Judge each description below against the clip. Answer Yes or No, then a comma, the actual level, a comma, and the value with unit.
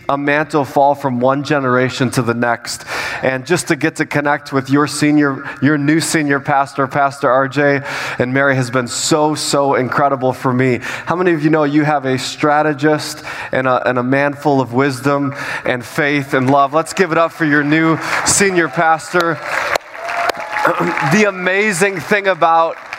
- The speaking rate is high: No, average, 175 wpm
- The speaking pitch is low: No, medium, 145 Hz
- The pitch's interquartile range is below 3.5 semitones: Yes, average, 2.7 semitones